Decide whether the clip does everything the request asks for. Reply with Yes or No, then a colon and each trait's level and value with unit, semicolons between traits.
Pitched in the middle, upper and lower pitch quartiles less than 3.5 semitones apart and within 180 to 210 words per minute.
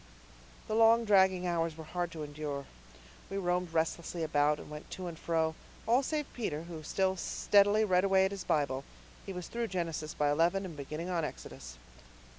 No: medium, 175 Hz; average, 3.8 semitones; average, 185 wpm